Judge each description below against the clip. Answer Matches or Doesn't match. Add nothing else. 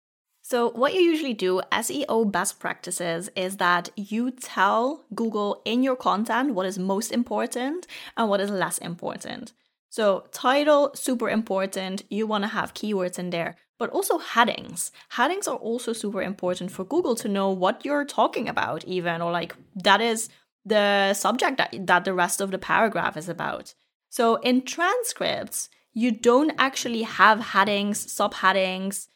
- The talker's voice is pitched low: Doesn't match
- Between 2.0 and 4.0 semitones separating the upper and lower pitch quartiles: Doesn't match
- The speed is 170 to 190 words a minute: Doesn't match